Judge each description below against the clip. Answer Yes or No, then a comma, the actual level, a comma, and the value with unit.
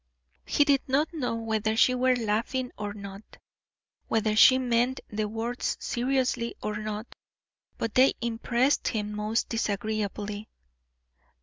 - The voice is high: Yes, high, 225 Hz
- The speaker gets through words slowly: Yes, slow, 125 wpm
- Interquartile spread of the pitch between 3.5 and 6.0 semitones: No, average, 3.1 semitones